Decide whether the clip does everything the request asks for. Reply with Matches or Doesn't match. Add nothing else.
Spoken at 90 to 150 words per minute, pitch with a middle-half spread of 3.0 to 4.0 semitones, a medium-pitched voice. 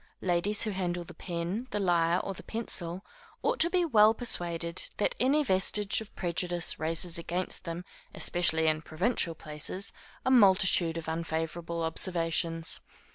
Matches